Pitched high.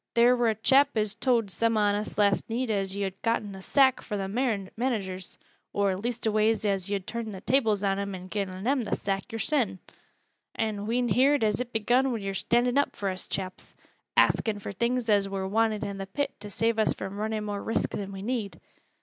Yes: high, 215 Hz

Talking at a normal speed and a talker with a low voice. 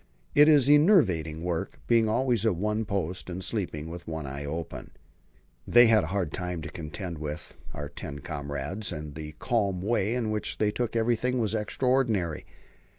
Yes: average, 170 wpm; very low, 95 Hz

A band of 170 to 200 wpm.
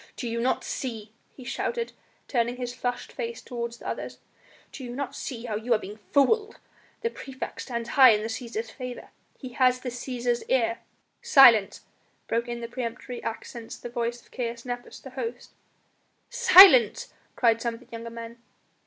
Yes: average, 180 wpm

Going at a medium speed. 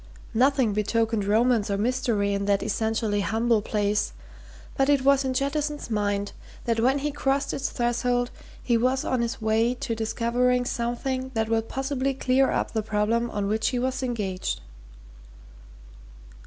Yes: average, 155 wpm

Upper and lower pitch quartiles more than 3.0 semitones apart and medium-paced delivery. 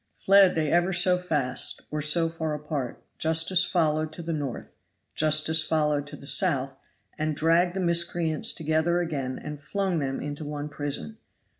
No: narrow, 2.6 semitones; average, 160 wpm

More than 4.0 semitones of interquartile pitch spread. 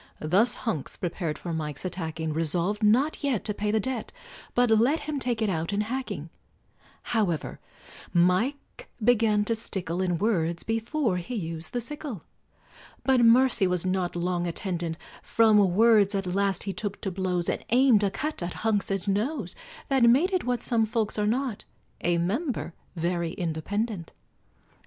Yes: average, 5.0 semitones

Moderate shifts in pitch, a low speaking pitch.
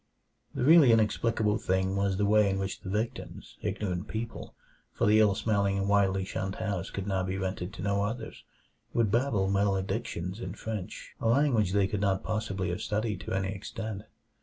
No: narrow, 2.2 semitones; low, 100 Hz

